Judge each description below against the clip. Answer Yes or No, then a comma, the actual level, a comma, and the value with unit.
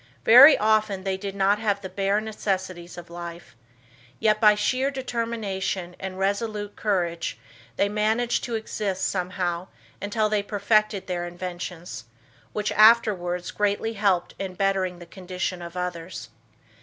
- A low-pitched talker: No, high, 195 Hz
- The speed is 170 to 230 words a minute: No, slow, 135 wpm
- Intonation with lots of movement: No, average, 2.9 semitones